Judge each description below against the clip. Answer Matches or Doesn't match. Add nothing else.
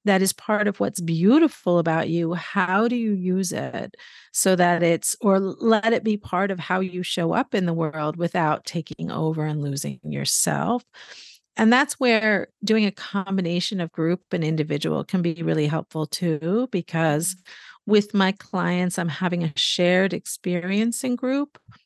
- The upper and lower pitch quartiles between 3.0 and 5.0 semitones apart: Matches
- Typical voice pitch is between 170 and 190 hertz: Matches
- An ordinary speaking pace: Matches